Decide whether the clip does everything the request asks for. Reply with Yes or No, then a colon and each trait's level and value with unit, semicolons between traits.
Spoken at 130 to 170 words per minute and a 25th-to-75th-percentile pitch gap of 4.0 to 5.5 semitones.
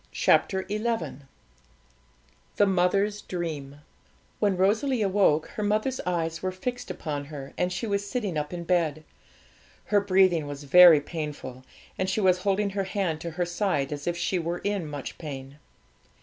Yes: average, 160 wpm; average, 4.6 semitones